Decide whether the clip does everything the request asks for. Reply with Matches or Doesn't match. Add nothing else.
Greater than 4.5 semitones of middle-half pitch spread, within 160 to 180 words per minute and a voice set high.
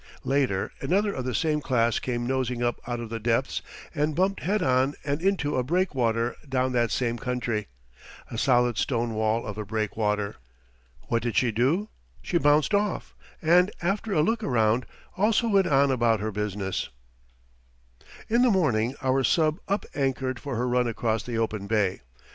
Doesn't match